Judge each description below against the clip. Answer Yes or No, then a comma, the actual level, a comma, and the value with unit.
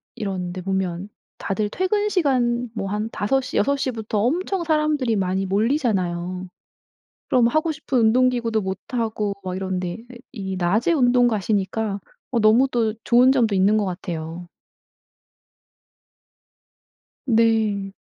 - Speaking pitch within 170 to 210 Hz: No, high, 220 Hz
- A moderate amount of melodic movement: Yes, average, 4.6 semitones